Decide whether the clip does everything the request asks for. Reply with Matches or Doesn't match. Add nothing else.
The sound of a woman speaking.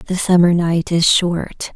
Matches